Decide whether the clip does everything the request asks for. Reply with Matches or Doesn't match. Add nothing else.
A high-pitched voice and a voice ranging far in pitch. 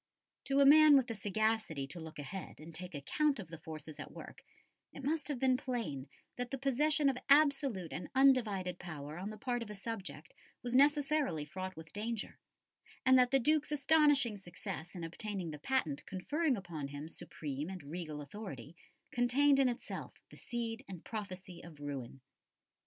Matches